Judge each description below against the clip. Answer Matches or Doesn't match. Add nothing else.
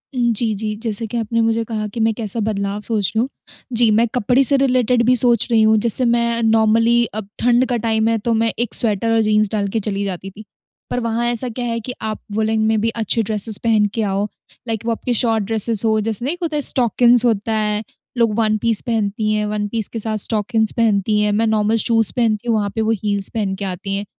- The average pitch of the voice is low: Doesn't match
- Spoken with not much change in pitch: Matches